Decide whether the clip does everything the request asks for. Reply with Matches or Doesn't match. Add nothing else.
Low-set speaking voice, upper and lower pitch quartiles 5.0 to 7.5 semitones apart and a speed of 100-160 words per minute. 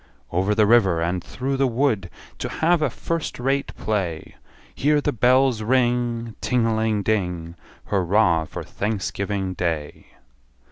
Matches